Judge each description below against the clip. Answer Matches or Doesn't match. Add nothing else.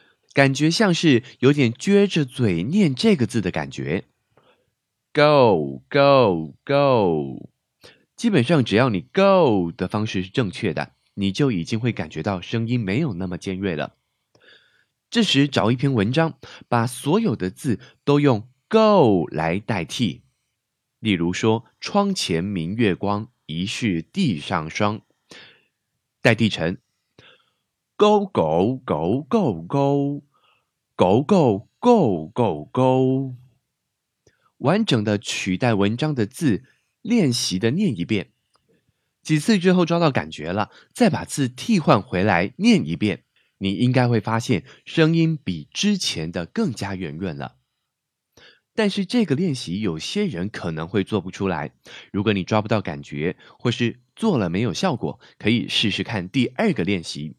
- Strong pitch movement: Matches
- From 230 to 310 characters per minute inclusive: Doesn't match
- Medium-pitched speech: Doesn't match